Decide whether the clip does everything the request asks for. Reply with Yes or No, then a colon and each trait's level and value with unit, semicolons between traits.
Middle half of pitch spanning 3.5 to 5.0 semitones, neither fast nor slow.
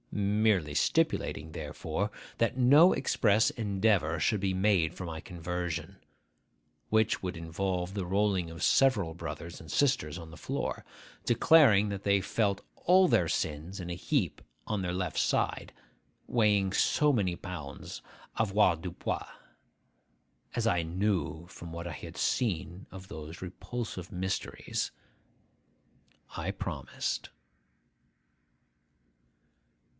No: average, 3.9 semitones; slow, 115 wpm